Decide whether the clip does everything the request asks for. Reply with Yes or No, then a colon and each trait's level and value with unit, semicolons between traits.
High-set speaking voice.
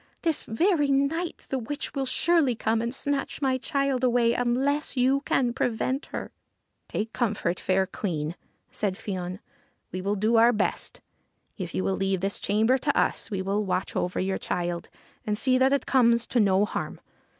Yes: high, 235 Hz